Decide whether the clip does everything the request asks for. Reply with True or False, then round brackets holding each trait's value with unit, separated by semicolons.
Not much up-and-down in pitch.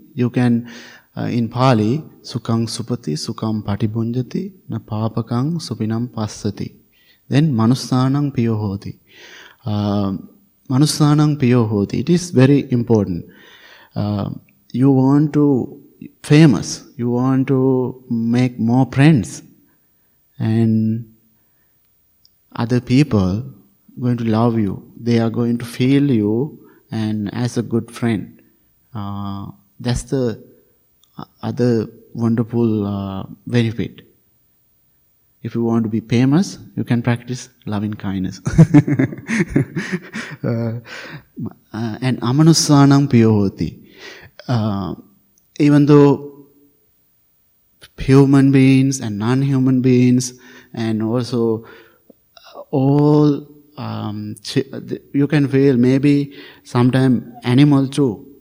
False (3.6 semitones)